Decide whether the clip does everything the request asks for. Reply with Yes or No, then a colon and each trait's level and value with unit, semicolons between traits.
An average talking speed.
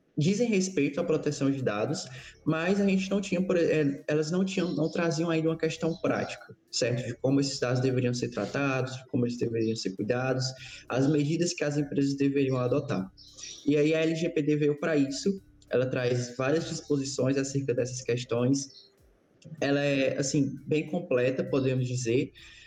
Yes: average, 160 wpm